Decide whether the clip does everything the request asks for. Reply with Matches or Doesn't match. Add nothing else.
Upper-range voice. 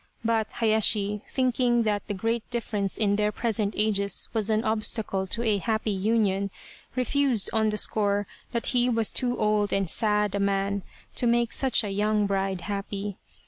Matches